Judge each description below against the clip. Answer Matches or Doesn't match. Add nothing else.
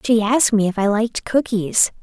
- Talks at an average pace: Doesn't match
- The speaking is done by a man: Doesn't match